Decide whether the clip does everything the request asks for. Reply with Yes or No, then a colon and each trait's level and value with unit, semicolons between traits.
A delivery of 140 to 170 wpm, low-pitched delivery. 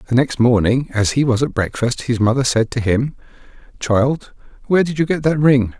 No: fast, 205 wpm; low, 130 Hz